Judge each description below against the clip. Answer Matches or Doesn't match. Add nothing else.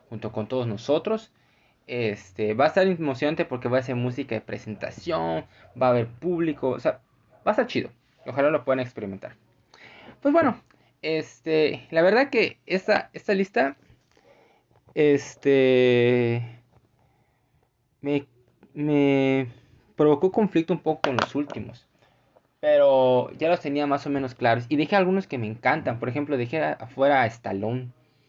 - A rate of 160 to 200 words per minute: Doesn't match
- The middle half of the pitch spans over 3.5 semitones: Matches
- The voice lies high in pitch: Doesn't match